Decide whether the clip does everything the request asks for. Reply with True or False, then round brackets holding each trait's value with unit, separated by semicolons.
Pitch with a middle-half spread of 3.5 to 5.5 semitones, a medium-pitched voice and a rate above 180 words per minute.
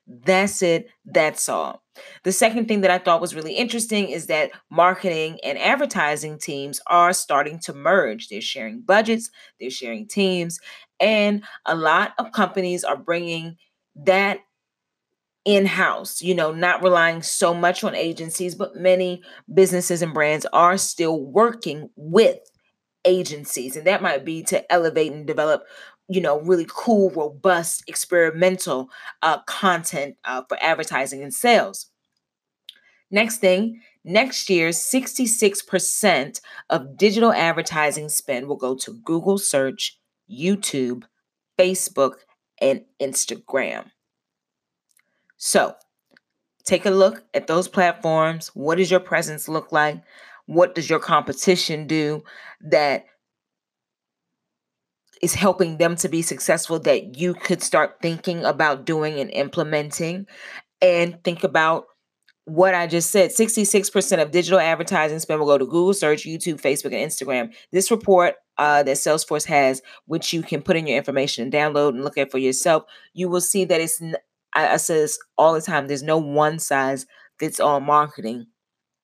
False (3.8 semitones; 170 Hz; 145 wpm)